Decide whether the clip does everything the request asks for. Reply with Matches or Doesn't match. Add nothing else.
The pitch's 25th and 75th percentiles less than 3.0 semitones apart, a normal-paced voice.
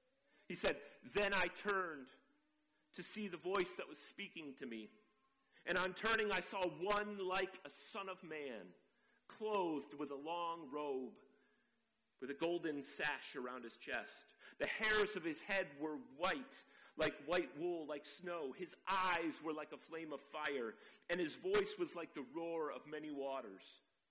Doesn't match